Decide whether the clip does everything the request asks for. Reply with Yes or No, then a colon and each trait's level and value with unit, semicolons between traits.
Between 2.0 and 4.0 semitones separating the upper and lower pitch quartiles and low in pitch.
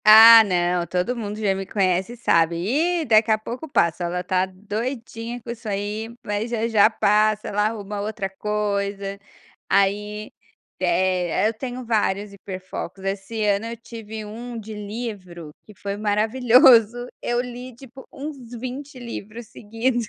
No: average, 2.8 semitones; high, 215 Hz